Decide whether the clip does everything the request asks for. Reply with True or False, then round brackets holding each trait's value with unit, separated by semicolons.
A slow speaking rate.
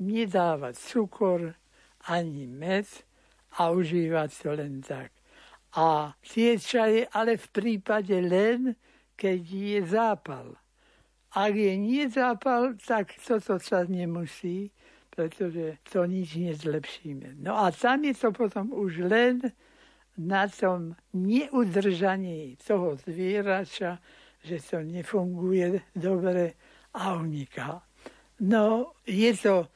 True (105 wpm)